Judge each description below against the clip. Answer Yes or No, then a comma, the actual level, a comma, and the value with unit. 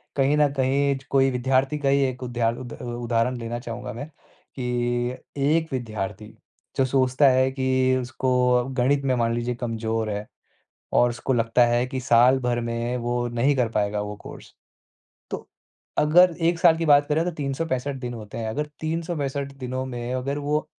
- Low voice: Yes, low, 130 Hz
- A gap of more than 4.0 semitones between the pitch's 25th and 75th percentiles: No, average, 2.8 semitones